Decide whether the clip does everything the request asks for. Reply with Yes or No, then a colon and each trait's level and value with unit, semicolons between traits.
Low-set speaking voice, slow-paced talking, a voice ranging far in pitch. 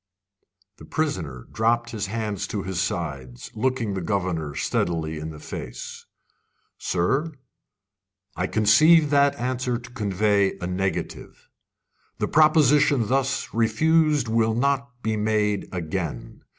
Yes: low, 110 Hz; slow, 120 wpm; wide, 6.1 semitones